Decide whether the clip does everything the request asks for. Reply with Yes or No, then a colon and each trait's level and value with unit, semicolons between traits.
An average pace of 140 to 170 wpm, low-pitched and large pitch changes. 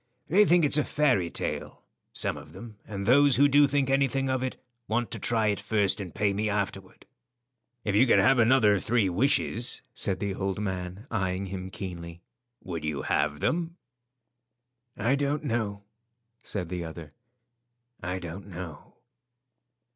Yes: average, 160 wpm; low, 105 Hz; wide, 6.0 semitones